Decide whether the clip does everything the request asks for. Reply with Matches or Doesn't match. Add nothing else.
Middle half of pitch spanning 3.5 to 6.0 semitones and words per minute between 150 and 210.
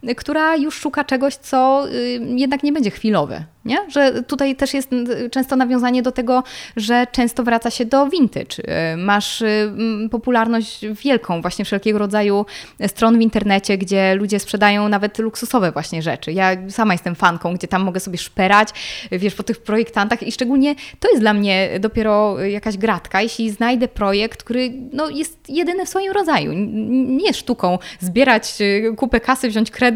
Matches